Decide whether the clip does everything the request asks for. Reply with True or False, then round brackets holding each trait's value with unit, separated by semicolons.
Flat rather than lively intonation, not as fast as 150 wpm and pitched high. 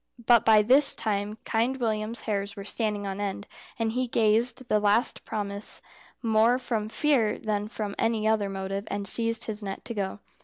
False (2.1 semitones; 180 wpm; 215 Hz)